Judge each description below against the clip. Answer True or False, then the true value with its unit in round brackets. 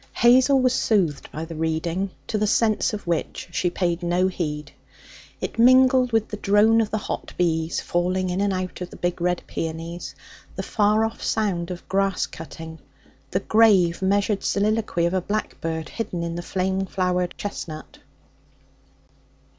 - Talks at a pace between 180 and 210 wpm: False (160 wpm)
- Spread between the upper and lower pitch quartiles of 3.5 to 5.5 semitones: True (3.8 semitones)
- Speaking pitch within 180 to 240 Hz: True (185 Hz)